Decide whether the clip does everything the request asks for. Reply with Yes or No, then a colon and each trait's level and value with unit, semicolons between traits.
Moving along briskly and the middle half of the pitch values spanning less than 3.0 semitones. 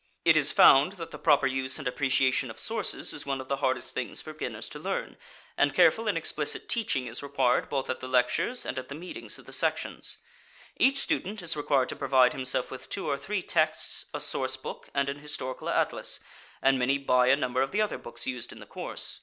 Yes: fast, 220 wpm; narrow, 2.6 semitones